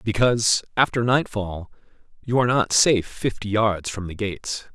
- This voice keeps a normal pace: Yes, average, 150 wpm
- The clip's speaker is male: Yes, male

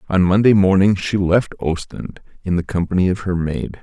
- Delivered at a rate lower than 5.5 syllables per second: Yes, 5.1 syllables/s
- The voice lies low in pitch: Yes, very low, 90 Hz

